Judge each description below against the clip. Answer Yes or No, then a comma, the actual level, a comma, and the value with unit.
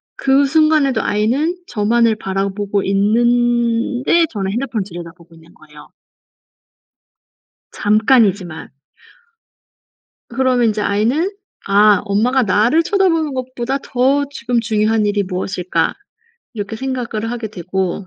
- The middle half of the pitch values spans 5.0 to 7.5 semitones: No, average, 4.4 semitones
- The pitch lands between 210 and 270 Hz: Yes, high, 225 Hz